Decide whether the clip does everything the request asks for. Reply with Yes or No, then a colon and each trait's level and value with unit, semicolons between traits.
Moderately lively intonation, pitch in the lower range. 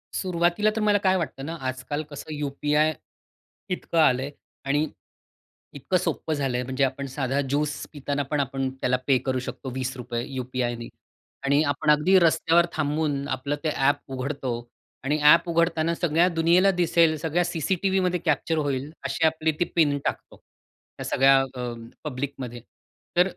No: average, 3.6 semitones; medium, 145 Hz